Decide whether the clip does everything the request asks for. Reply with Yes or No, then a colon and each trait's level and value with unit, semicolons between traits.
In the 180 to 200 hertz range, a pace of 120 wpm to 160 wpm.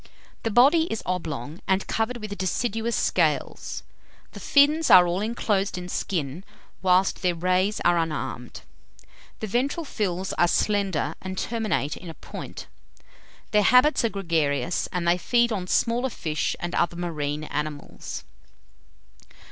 Yes: medium, 185 Hz; average, 140 wpm